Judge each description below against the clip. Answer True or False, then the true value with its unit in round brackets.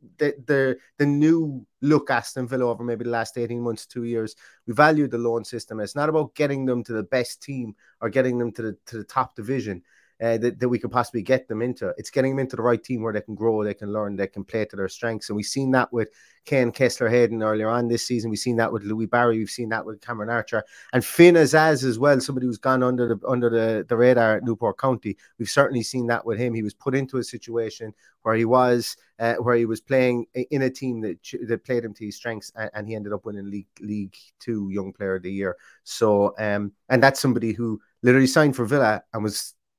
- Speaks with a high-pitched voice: False (120 Hz)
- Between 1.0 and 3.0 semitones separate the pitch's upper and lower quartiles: True (2.7 semitones)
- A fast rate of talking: True (245 wpm)